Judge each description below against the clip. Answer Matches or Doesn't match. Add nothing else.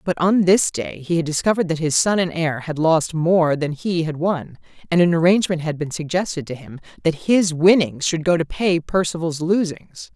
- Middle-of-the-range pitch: Matches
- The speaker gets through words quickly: Matches